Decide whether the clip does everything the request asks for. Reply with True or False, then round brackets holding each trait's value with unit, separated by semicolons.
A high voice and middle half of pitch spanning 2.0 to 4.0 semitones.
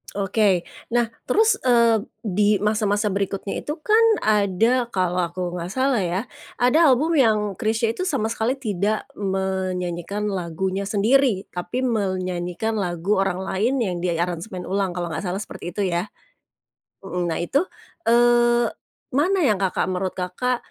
False (205 Hz; 4.5 semitones)